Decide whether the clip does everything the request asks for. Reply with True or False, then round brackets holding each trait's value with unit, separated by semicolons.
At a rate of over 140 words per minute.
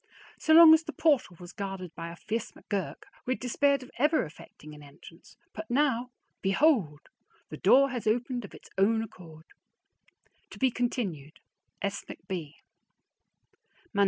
True (150 wpm)